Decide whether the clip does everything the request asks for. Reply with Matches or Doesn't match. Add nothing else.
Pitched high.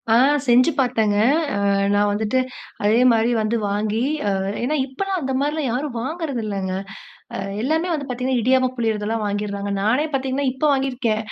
Matches